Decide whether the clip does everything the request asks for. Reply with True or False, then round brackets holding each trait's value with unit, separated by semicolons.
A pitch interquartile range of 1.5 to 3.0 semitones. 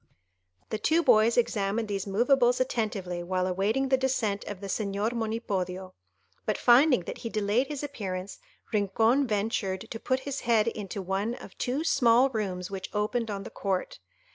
False (3.8 semitones)